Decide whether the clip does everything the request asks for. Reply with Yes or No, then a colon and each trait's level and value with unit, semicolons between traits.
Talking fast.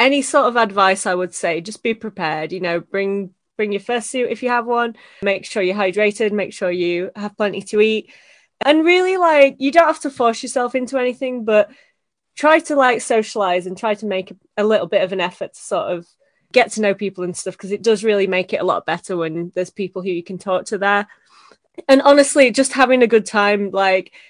Yes: fast, 230 wpm